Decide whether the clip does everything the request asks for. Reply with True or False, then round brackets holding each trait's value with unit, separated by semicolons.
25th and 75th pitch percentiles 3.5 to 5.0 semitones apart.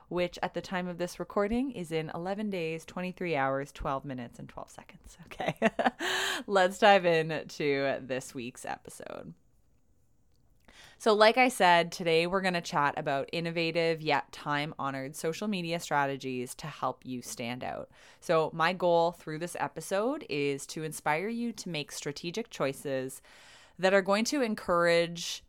True (4.6 semitones)